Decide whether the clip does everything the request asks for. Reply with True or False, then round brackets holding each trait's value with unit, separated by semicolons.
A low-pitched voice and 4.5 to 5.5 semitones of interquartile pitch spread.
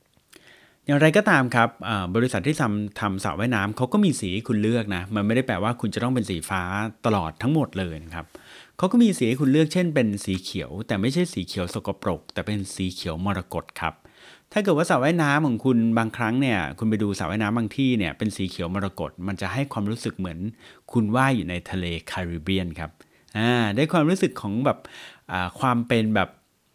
True (110 Hz; 4.9 semitones)